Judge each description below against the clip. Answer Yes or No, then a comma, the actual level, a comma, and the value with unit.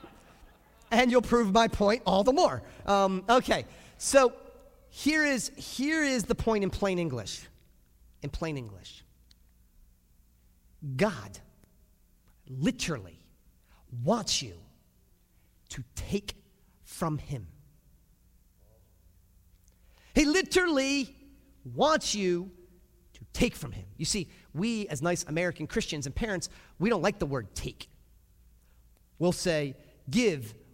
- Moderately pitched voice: Yes, medium, 170 Hz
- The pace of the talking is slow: Yes, slow, 110 wpm